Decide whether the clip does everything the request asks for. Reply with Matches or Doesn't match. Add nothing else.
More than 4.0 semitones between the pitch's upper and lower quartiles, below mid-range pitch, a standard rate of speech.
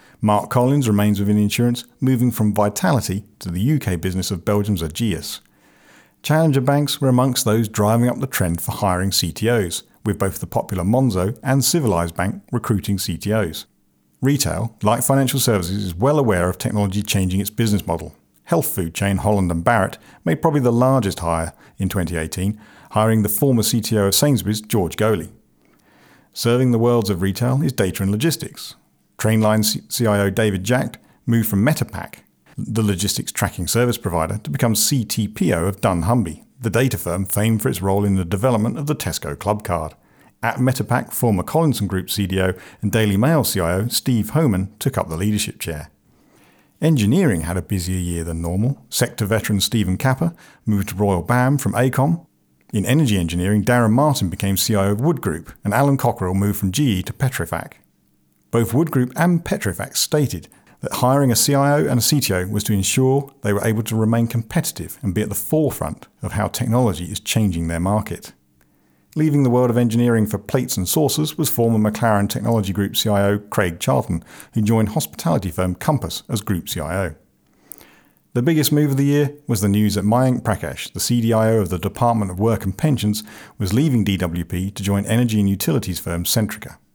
Matches